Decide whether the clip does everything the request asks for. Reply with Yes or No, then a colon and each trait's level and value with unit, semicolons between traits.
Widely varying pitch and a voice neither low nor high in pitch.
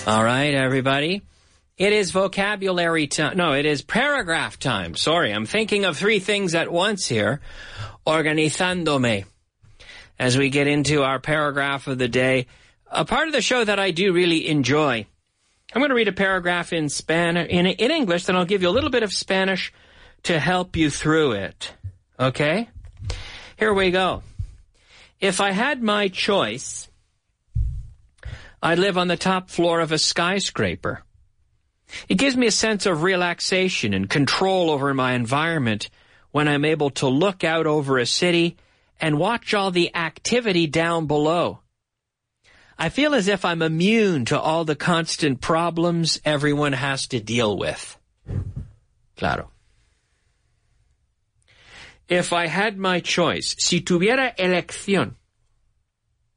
Yes: wide, 6.1 semitones; medium, 160 Hz